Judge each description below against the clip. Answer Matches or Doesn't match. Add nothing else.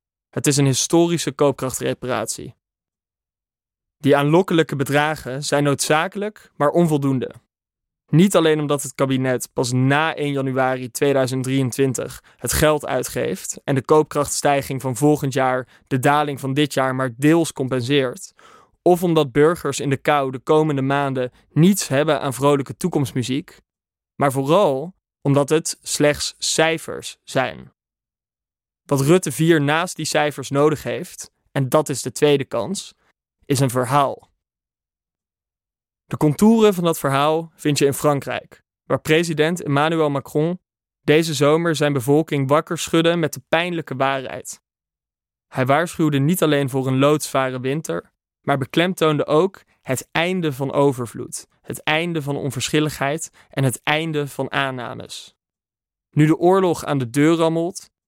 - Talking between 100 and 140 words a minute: Matches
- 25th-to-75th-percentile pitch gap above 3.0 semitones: Doesn't match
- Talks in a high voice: Doesn't match